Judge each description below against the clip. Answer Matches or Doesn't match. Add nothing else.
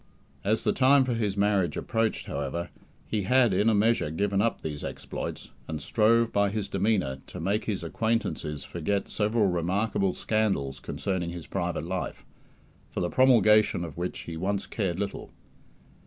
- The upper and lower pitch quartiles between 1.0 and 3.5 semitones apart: Doesn't match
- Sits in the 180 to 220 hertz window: Doesn't match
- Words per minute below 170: Matches